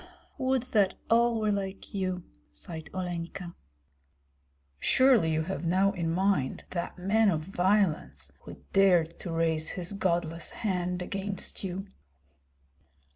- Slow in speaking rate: Yes, slow, 125 wpm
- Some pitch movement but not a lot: Yes, average, 3.0 semitones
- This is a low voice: No, medium, 185 Hz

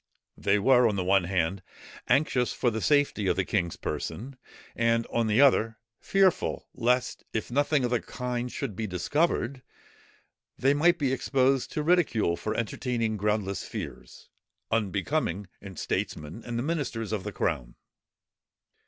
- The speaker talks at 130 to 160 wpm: Yes, average, 150 wpm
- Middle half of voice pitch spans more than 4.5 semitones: Yes, average, 5.0 semitones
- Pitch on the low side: Yes, low, 115 Hz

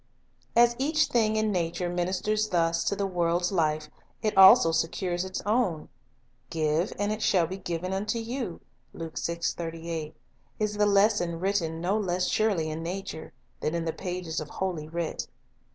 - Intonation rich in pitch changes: No, average, 3.9 semitones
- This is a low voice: No, medium, 185 Hz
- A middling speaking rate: Yes, average, 155 wpm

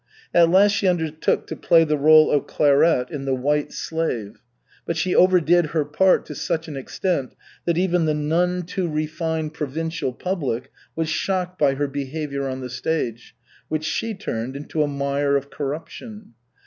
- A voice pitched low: No, medium, 155 Hz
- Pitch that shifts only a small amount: No, average, 3.5 semitones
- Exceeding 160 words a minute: Yes, average, 170 wpm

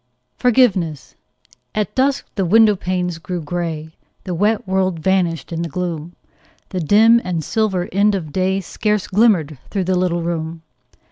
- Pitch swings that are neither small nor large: Yes, average, 3.5 semitones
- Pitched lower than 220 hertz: Yes, medium, 185 Hz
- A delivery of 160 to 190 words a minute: No, average, 150 wpm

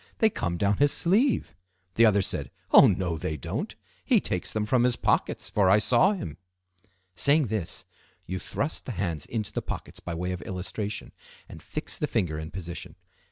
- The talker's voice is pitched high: No, low, 100 Hz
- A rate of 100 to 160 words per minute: No, average, 185 wpm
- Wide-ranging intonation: Yes, wide, 5.8 semitones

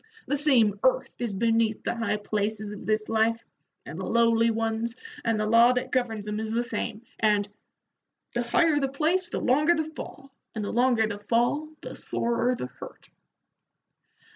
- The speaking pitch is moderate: No, high, 230 Hz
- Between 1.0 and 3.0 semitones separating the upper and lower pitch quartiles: Yes, average, 2.7 semitones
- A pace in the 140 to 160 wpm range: No, average, 175 wpm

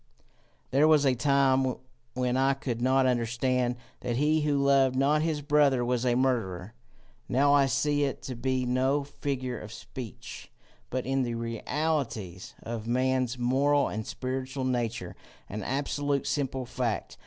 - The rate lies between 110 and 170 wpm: Yes, average, 150 wpm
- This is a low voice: Yes, low, 130 Hz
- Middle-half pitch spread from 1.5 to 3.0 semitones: Yes, narrow, 2.4 semitones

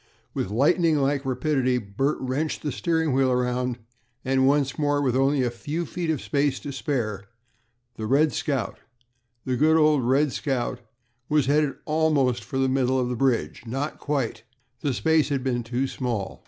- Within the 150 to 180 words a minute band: Yes, average, 170 wpm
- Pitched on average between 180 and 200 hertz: No, low, 135 Hz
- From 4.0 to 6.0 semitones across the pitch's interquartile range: No, average, 2.8 semitones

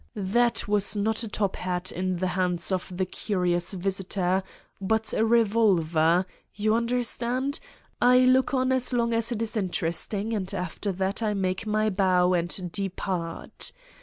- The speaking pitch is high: Yes, high, 200 Hz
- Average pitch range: Yes, average, 3.7 semitones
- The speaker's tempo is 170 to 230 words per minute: No, average, 160 wpm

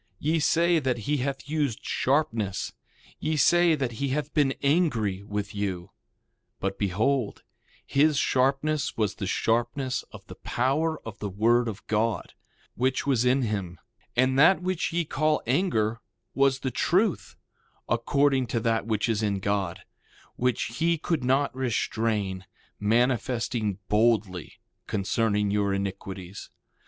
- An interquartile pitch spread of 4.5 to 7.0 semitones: Yes, average, 5.2 semitones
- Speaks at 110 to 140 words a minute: Yes, slow, 135 wpm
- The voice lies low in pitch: Yes, low, 120 Hz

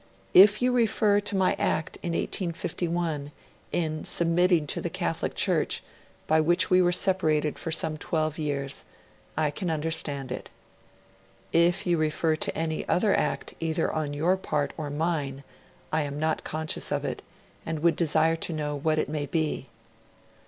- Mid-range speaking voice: Yes, medium, 160 Hz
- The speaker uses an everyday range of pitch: No, narrow, 2.3 semitones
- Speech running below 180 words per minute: Yes, average, 160 wpm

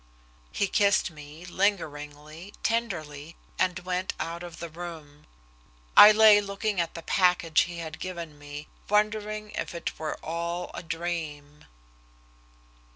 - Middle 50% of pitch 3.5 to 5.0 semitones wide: Yes, average, 4.2 semitones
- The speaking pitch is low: No, medium, 170 Hz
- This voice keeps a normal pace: No, slow, 130 wpm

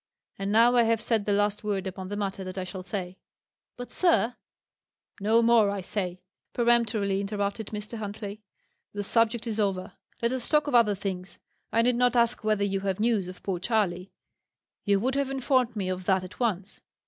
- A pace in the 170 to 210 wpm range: Yes, average, 195 wpm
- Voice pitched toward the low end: No, high, 210 Hz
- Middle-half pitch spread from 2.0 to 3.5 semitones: Yes, average, 3.2 semitones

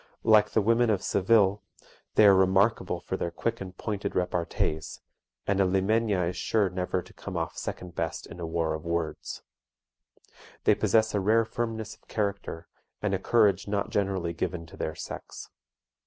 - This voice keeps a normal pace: Yes, average, 170 wpm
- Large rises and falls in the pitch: No, average, 3.5 semitones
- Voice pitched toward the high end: No, very low, 95 Hz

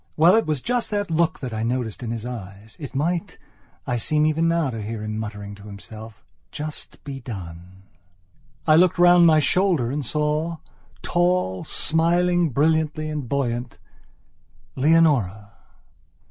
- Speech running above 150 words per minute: No, average, 145 wpm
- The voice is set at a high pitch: No, medium, 145 Hz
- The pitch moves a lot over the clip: Yes, wide, 6.7 semitones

